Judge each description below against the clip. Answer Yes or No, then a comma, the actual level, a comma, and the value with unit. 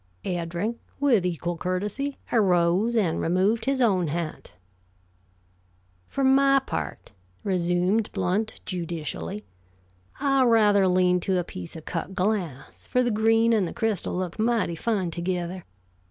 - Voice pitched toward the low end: No, high, 190 Hz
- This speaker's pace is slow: Yes, slow, 130 wpm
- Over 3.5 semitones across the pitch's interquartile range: Yes, average, 4.5 semitones